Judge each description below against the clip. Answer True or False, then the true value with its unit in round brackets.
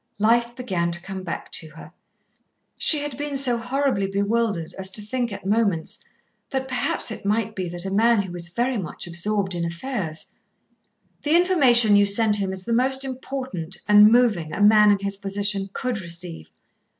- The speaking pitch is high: True (210 Hz)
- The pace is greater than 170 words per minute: True (180 wpm)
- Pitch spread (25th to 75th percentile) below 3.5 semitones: False (4.3 semitones)